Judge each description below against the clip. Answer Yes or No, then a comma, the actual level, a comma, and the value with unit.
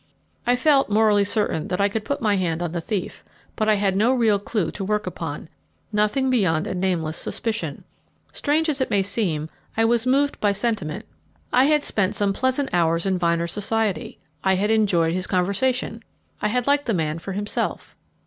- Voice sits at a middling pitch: No, high, 205 Hz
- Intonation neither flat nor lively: Yes, average, 4.3 semitones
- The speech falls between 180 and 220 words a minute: Yes, average, 190 wpm